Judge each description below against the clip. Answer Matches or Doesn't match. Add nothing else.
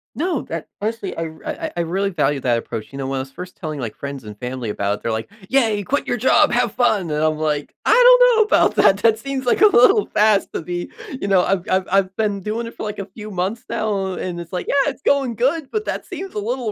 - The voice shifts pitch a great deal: Matches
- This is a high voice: Matches